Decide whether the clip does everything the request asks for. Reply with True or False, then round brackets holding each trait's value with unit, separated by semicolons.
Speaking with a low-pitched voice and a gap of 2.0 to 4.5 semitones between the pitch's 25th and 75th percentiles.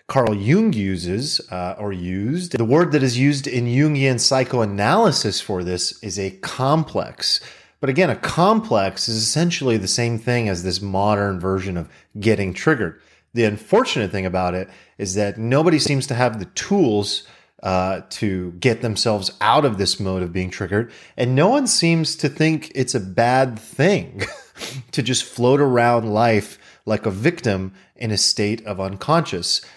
False (110 Hz; 5.5 semitones)